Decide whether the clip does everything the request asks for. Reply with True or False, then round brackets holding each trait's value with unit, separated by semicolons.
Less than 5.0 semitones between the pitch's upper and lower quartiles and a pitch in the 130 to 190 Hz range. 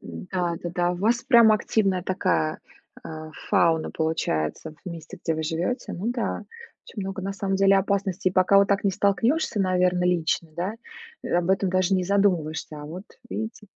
True (2.7 semitones; 185 Hz)